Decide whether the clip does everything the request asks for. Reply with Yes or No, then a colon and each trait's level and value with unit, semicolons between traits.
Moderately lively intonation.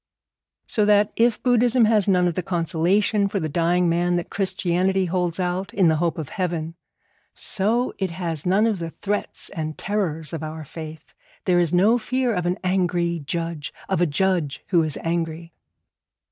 Yes: average, 3.2 semitones